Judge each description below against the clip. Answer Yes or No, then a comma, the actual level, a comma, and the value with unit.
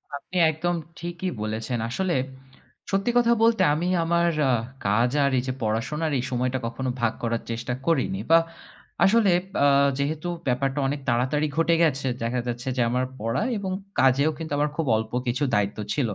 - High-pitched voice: No, medium, 140 Hz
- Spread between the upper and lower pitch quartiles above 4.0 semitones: Yes, wide, 5.6 semitones